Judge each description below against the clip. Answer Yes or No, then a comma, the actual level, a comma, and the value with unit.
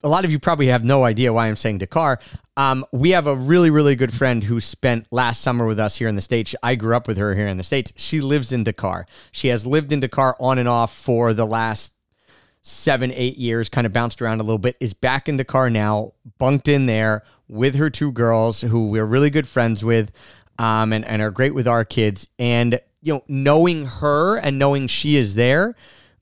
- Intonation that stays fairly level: No, average, 3.4 semitones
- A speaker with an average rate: No, fast, 230 wpm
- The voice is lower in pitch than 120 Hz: No, low, 125 Hz